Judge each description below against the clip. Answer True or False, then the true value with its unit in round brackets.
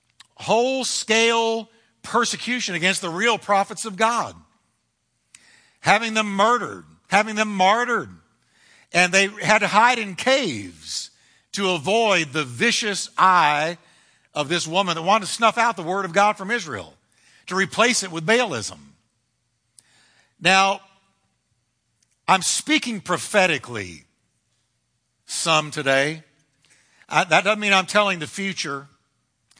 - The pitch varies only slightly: False (5.0 semitones)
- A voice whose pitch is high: True (195 Hz)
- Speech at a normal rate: False (120 wpm)